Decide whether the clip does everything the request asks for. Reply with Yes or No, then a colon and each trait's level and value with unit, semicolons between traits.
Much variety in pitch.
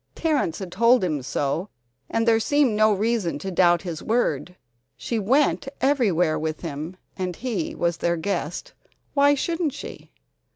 Yes: wide, 6.0 semitones